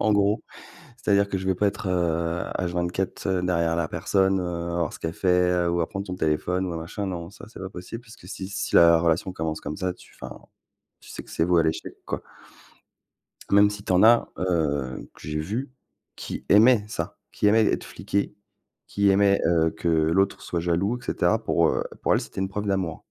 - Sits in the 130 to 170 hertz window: No, very low, 90 Hz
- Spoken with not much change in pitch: No, average, 3.0 semitones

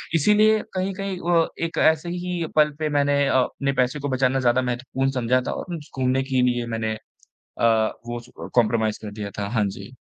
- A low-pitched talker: Yes, low, 130 Hz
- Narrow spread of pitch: No, average, 4.7 semitones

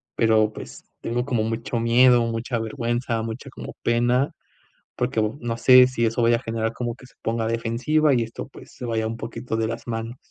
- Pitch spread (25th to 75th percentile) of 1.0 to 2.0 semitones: Yes, narrow, 1.5 semitones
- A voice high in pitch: No, low, 115 Hz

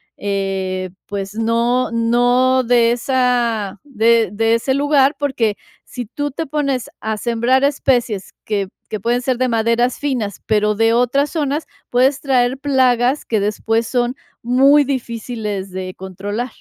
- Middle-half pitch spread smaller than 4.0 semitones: Yes, average, 3.3 semitones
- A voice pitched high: Yes, high, 240 Hz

